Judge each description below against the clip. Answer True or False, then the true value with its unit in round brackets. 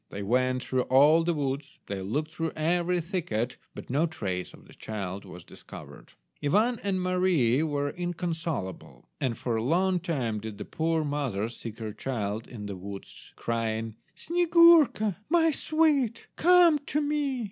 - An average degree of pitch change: False (8.6 semitones)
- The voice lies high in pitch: False (150 Hz)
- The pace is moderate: True (160 wpm)